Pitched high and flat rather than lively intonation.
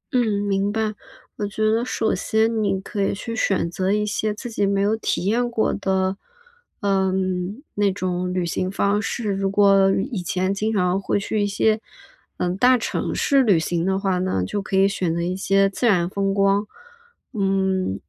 Yes: high, 195 Hz; narrow, 1.9 semitones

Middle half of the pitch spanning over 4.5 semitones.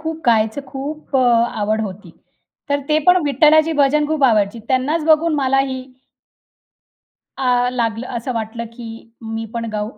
Yes: average, 4.9 semitones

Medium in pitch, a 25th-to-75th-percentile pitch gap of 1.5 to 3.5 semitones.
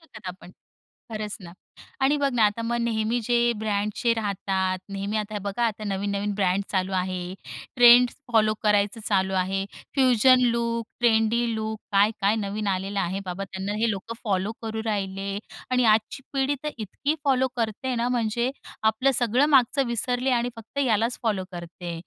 No: high, 215 Hz; average, 3.2 semitones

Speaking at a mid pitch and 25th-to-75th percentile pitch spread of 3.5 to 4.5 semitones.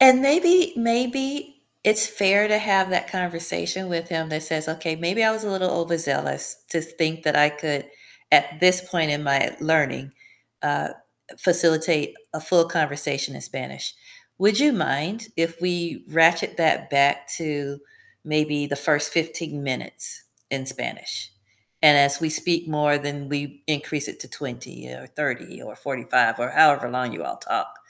Yes: medium, 160 Hz; average, 4.0 semitones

